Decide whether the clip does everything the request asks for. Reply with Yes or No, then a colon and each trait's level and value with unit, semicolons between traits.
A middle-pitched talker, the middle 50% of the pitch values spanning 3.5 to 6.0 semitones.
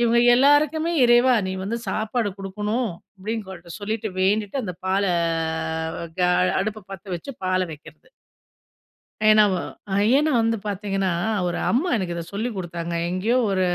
No: high, 210 Hz; average, 4.0 semitones